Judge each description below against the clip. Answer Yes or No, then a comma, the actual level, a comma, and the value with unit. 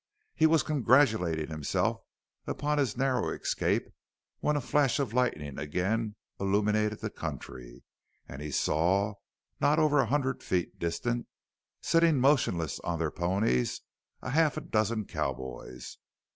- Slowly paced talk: Yes, slow, 130 wpm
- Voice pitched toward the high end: No, low, 105 Hz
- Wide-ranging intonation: Yes, wide, 8.9 semitones